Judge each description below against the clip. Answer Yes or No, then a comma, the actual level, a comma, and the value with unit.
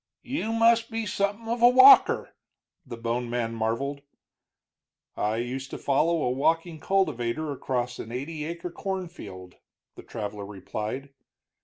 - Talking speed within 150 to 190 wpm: No, slow, 135 wpm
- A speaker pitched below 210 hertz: Yes, medium, 140 Hz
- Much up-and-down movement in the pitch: Yes, wide, 8.3 semitones